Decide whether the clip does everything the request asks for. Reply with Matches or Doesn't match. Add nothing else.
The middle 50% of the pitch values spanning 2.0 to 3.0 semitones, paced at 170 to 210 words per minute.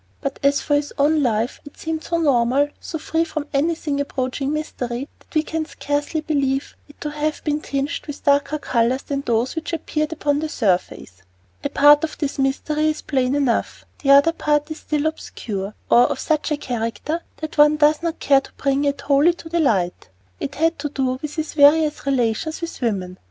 Matches